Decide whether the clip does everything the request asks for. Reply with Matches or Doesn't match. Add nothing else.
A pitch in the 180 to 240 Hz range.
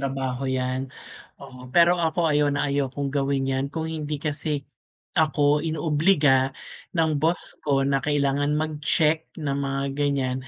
Doesn't match